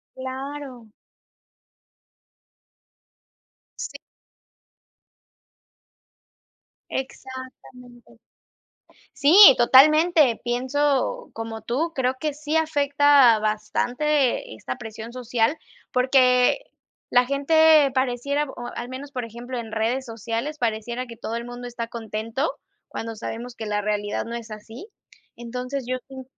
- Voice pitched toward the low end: No, very high, 250 Hz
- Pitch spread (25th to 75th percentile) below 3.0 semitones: No, average, 3.3 semitones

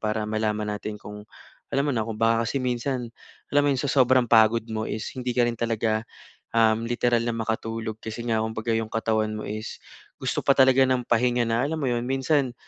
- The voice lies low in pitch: Yes, low, 115 Hz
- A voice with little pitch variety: Yes, narrow, 2.2 semitones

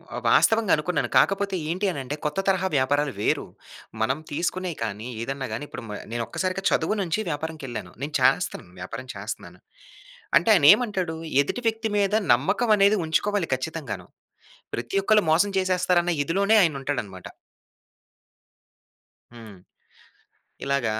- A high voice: No, medium, 160 Hz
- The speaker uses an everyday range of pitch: No, wide, 6.3 semitones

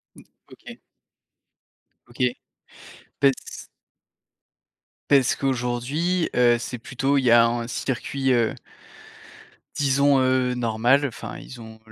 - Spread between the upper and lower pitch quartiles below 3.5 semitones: Yes, narrow, 2.4 semitones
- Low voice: Yes, low, 125 Hz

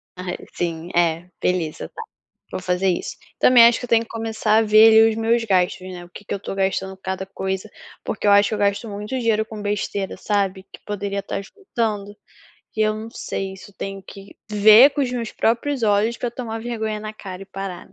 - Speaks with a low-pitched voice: No, high, 205 Hz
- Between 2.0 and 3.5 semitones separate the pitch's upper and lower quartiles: Yes, narrow, 2.6 semitones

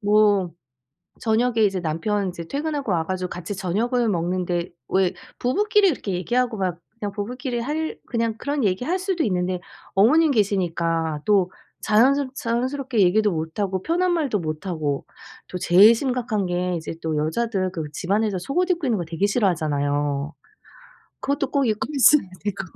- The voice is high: Yes, high, 205 Hz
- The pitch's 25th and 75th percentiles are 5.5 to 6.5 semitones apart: Yes, wide, 5.9 semitones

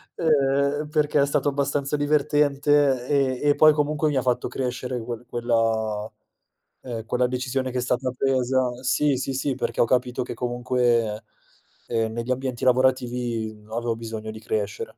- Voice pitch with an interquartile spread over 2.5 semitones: Yes, average, 2.9 semitones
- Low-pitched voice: Yes, low, 125 Hz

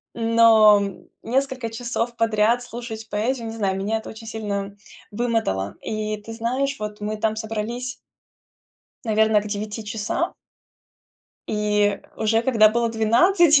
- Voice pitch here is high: Yes, high, 220 Hz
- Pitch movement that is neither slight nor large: No, narrow, 1.9 semitones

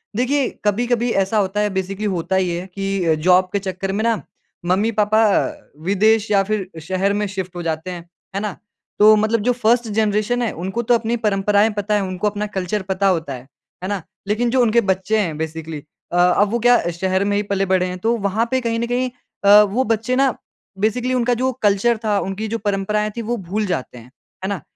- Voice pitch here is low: No, high, 205 Hz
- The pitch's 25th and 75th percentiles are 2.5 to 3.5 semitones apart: Yes, average, 3.0 semitones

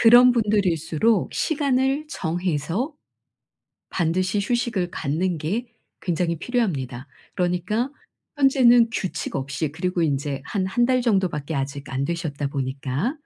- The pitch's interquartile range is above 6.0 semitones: Yes, wide, 7.9 semitones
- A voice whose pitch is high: No, medium, 180 Hz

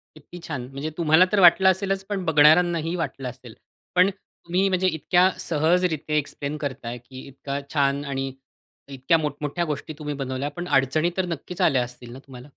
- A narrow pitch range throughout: No, average, 4.4 semitones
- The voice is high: No, medium, 150 Hz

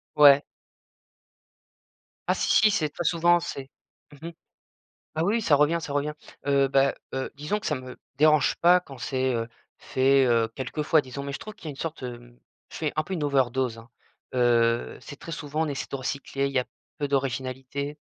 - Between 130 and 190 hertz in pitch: Yes, medium, 140 Hz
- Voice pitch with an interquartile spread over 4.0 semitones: No, average, 3.0 semitones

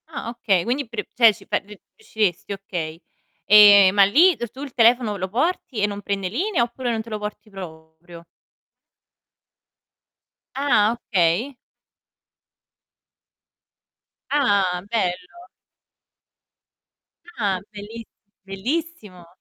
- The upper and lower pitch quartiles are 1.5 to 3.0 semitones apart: No, average, 4.1 semitones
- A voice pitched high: Yes, high, 210 Hz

